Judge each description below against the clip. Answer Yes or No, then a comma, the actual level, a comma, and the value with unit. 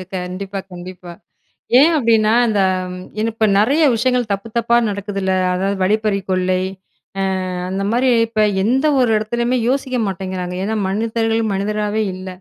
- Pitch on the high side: Yes, high, 210 Hz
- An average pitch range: Yes, average, 3.3 semitones